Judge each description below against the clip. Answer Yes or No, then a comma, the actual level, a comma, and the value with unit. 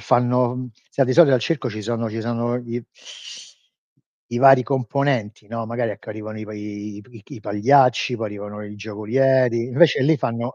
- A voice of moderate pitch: No, low, 115 Hz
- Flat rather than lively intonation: No, average, 3.1 semitones